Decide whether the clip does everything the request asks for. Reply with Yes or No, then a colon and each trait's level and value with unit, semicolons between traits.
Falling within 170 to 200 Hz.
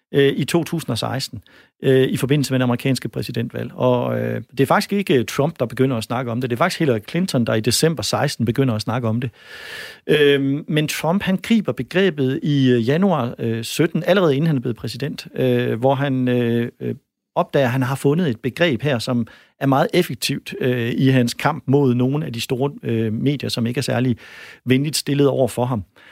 No: low, 130 Hz